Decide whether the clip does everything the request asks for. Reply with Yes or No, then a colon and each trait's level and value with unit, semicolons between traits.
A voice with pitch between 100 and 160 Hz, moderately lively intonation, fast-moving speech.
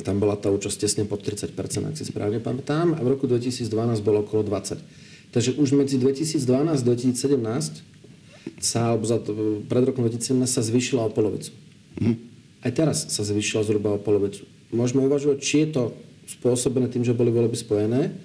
Yes: low, 120 Hz; average, 4.4 semitones; fast, 175 wpm